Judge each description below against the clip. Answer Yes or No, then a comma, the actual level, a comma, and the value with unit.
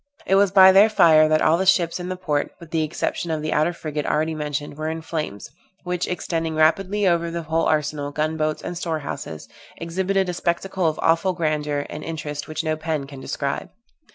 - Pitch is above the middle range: No, medium, 160 Hz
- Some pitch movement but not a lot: No, narrow, 2.3 semitones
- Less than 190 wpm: No, fast, 205 wpm